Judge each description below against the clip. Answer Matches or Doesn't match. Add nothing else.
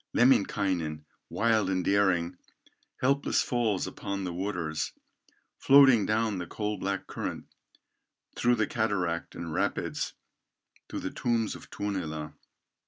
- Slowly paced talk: Matches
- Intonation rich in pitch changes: Doesn't match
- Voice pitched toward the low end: Matches